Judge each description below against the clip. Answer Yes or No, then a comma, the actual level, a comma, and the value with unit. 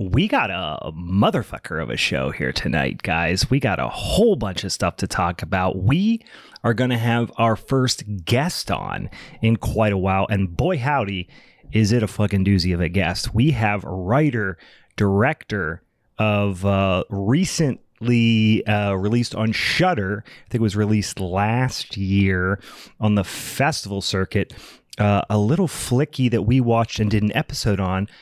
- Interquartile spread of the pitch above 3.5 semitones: Yes, average, 4.1 semitones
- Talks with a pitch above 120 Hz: No, low, 105 Hz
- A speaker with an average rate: Yes, average, 170 wpm